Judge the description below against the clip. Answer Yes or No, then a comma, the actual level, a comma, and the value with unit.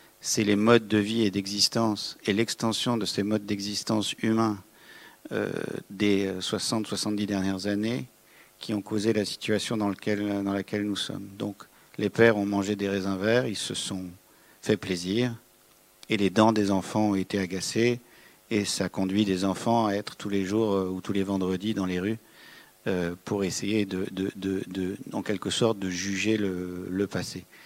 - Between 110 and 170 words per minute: No, average, 180 wpm